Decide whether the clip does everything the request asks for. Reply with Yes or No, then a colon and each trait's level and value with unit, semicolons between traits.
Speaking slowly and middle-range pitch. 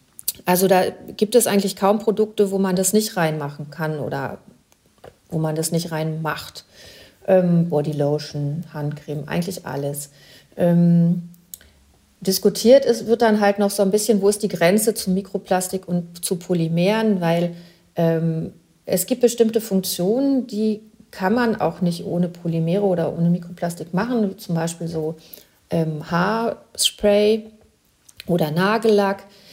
No: average, 140 wpm; medium, 180 Hz